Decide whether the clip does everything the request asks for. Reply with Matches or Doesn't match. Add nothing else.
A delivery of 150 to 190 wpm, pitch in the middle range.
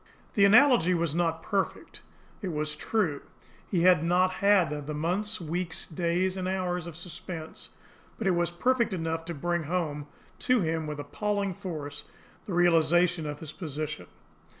Matches